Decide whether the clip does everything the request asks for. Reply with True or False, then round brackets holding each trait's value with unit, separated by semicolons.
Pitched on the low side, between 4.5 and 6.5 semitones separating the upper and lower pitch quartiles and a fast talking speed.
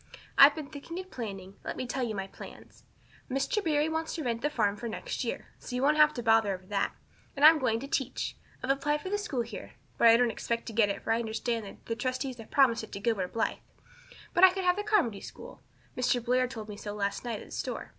False (245 Hz; 4.9 semitones; 250 wpm)